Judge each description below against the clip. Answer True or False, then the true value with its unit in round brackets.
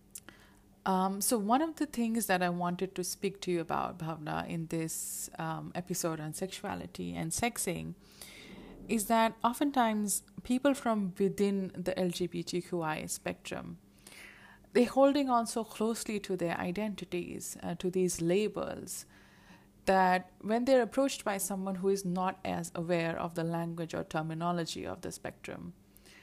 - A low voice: False (185 Hz)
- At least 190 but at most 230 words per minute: False (145 wpm)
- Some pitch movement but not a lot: True (4.1 semitones)